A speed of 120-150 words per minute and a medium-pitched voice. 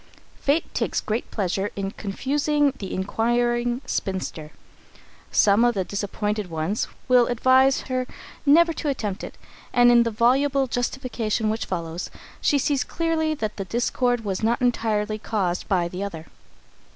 No: average, 145 wpm; high, 230 Hz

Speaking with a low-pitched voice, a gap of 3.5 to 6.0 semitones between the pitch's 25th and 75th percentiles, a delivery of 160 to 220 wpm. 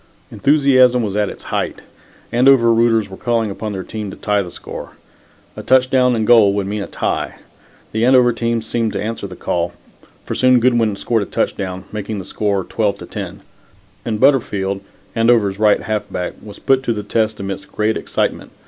No: low, 110 Hz; average, 3.0 semitones; average, 185 wpm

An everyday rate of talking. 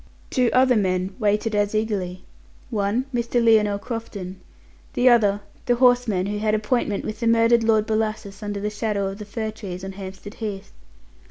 Yes: average, 170 wpm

